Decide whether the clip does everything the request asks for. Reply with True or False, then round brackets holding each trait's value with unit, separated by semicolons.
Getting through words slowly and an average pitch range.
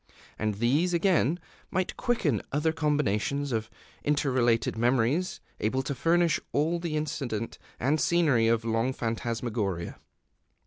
False (125 wpm; 5.8 semitones)